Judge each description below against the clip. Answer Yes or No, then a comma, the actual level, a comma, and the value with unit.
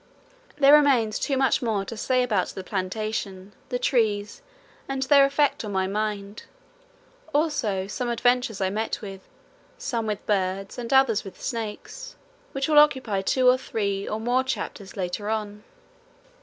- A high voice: Yes, high, 220 Hz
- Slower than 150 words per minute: No, average, 155 wpm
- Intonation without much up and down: No, average, 4.4 semitones